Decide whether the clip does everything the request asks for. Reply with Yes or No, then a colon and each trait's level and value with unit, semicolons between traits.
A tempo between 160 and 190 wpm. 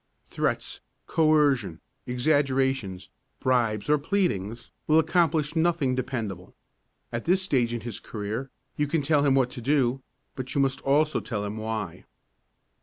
No: average, 140 wpm